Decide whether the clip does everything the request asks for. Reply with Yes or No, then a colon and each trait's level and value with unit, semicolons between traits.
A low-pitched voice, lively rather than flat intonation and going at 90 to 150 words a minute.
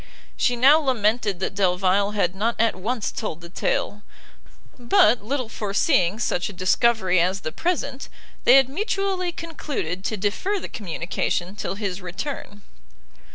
No: high, 210 Hz; wide, 5.7 semitones; average, 145 wpm